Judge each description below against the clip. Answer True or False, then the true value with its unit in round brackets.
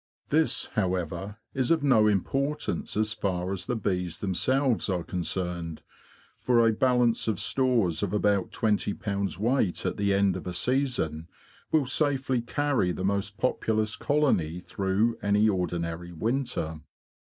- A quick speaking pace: False (140 wpm)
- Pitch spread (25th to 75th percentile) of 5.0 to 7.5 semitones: True (5.5 semitones)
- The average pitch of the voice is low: True (105 Hz)